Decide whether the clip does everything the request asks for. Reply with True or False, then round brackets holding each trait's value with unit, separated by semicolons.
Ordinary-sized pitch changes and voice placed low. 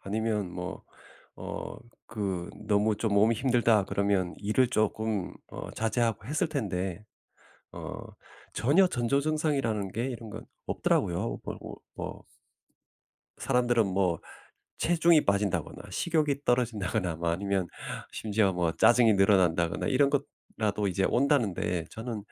True (4.2 semitones; 110 Hz)